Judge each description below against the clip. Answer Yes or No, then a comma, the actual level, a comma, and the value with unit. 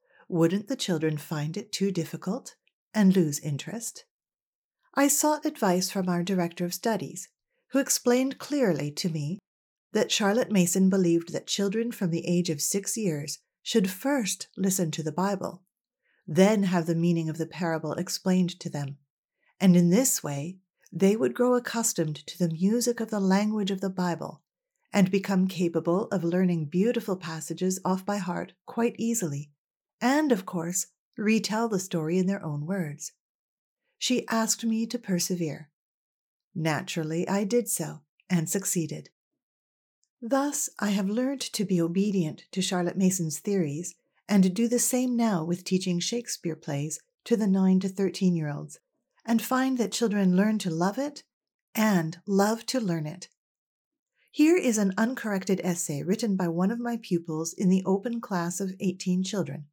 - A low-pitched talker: No, high, 190 Hz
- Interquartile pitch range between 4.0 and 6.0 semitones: Yes, average, 4.7 semitones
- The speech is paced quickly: No, average, 160 wpm